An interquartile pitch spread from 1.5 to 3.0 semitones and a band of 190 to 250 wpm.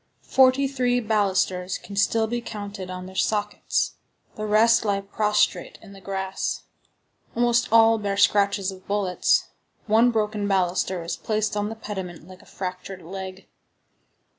No: narrow, 2.6 semitones; average, 145 wpm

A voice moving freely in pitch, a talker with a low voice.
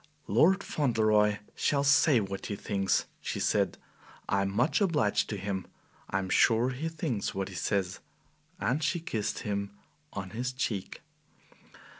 Yes: wide, 5.7 semitones; low, 110 Hz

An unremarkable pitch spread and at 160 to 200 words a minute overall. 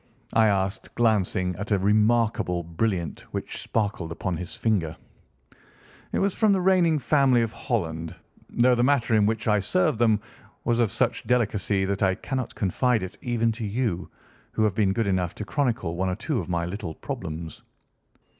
Yes: average, 4.4 semitones; average, 175 wpm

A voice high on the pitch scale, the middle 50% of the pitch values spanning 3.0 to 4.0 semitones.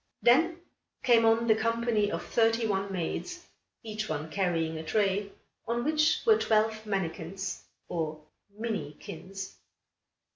Yes: high, 215 Hz; average, 3.6 semitones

